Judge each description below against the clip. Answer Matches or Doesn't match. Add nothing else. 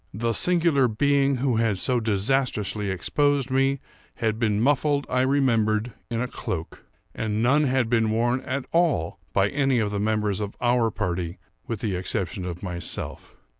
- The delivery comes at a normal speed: Matches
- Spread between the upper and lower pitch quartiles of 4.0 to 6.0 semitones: Matches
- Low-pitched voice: Matches